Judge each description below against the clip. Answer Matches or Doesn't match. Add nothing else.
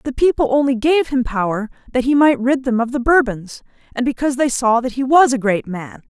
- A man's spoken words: Doesn't match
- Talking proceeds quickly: Matches